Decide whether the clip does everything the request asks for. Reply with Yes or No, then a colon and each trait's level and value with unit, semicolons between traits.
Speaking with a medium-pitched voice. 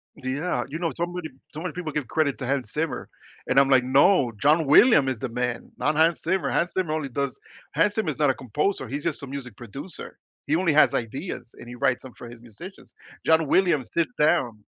Yes: medium, 145 Hz